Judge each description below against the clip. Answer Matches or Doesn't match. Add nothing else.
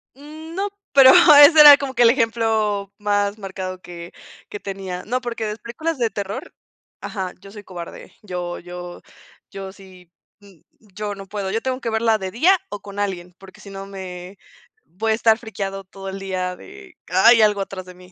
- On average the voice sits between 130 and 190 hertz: Doesn't match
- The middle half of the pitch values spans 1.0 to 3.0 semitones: Doesn't match